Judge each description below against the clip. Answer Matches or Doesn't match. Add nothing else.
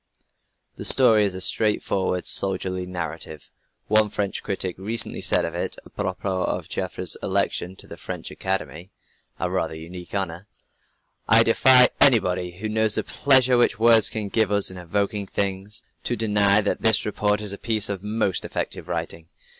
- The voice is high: Doesn't match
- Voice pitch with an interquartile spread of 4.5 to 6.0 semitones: Doesn't match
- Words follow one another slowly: Doesn't match